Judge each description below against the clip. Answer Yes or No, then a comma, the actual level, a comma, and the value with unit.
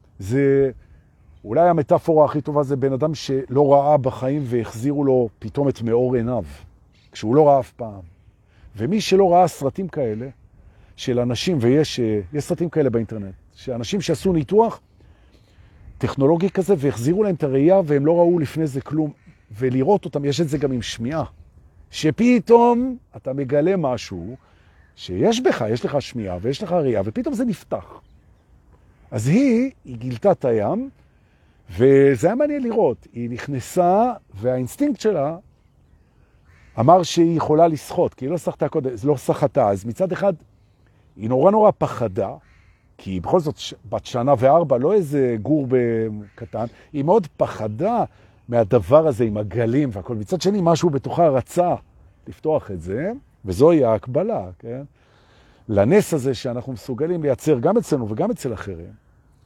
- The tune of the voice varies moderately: No, wide, 6.7 semitones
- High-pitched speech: No, low, 135 Hz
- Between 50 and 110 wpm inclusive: No, average, 145 wpm